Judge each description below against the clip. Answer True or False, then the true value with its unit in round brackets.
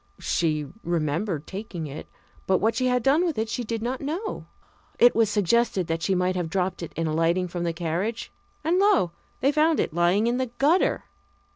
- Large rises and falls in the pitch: True (6.6 semitones)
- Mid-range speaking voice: False (195 Hz)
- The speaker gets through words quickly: False (195 wpm)